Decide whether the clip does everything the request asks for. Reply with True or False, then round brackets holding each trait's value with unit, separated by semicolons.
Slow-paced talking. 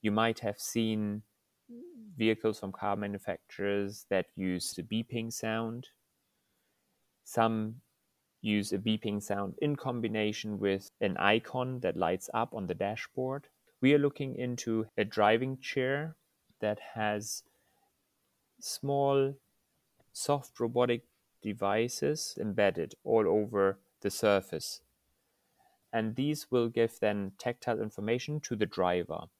True (115 wpm)